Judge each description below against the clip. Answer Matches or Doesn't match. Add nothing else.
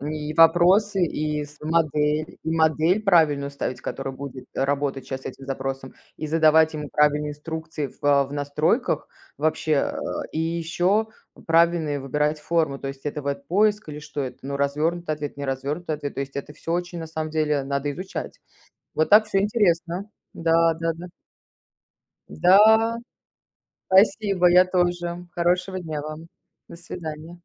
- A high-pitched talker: Doesn't match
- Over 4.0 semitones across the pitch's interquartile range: Doesn't match